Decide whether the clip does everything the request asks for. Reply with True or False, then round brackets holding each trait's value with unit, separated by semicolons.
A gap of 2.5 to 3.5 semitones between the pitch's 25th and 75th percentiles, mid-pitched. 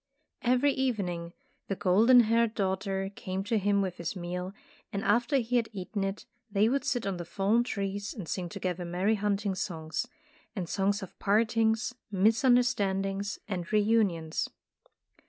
False (3.1 semitones; 200 Hz)